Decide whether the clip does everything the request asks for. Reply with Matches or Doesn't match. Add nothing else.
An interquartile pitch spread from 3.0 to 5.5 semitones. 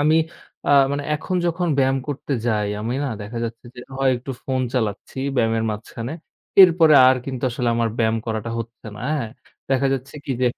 Matches